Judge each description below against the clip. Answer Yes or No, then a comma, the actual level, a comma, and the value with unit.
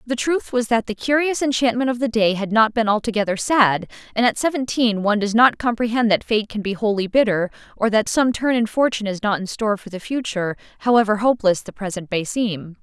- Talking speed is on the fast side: Yes, fast, 220 wpm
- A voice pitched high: Yes, high, 220 Hz